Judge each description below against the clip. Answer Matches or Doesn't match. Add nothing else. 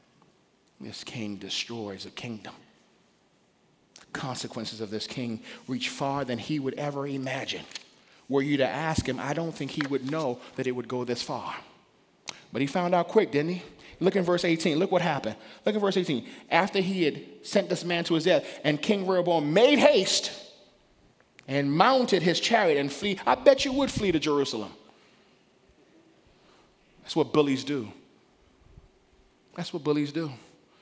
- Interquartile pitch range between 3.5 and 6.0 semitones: Matches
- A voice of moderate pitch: Matches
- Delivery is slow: Doesn't match